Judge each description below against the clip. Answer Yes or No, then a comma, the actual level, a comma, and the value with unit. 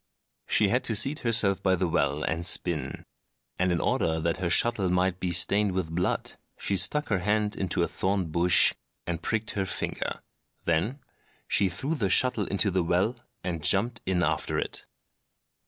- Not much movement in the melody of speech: No, average, 3.4 semitones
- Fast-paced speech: No, average, 175 wpm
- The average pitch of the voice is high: No, very low, 95 Hz